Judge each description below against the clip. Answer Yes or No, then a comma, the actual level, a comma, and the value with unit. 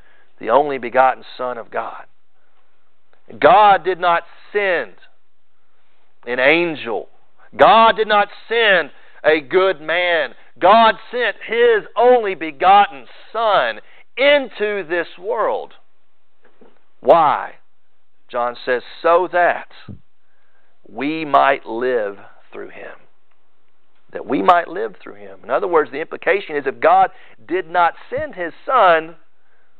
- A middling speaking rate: No, slow, 115 wpm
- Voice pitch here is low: No, high, 195 Hz